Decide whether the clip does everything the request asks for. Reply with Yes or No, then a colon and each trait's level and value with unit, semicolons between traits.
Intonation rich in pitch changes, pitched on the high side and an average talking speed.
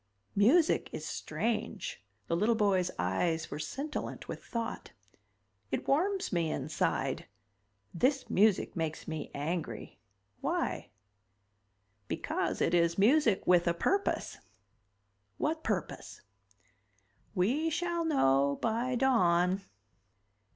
No: wide, 7.9 semitones; high, 200 Hz; slow, 100 wpm